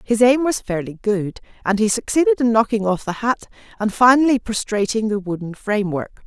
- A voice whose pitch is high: Yes, high, 220 Hz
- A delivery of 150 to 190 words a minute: Yes, average, 180 wpm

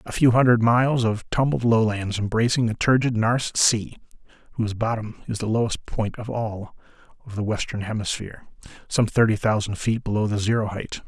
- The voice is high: No, low, 110 Hz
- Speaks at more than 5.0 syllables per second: Yes, 5.5 syllables/s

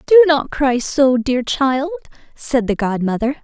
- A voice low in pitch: No, very high, 270 Hz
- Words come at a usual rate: Yes, average, 155 wpm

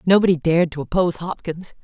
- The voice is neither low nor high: Yes, medium, 170 Hz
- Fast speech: No, average, 165 wpm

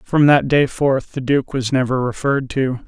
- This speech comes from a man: Yes, male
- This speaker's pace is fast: Yes, fast, 210 wpm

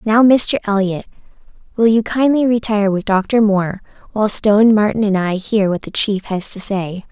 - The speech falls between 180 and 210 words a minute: Yes, average, 185 wpm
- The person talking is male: No, female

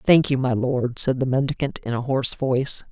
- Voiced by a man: No, female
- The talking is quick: Yes, fast, 225 wpm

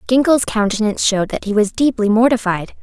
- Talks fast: No, average, 170 wpm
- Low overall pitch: No, high, 220 Hz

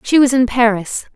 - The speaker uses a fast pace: Yes, fast, 210 wpm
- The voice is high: Yes, high, 245 Hz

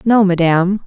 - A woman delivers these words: Yes, female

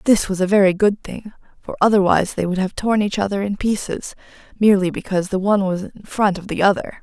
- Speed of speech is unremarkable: No, fast, 220 wpm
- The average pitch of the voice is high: Yes, high, 195 Hz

